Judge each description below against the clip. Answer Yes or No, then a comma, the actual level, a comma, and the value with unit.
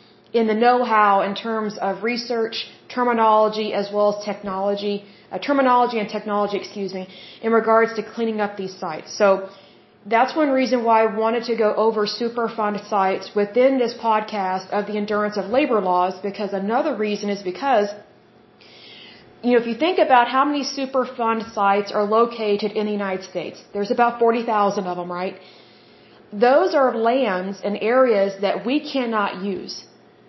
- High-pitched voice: Yes, high, 215 Hz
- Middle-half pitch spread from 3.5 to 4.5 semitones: No, average, 2.7 semitones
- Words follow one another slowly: No, average, 160 wpm